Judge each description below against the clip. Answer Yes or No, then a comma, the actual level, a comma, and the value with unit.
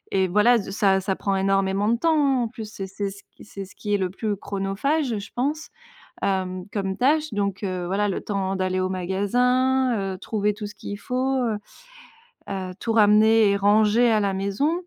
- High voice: Yes, high, 205 Hz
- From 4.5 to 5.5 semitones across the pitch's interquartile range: No, average, 3.4 semitones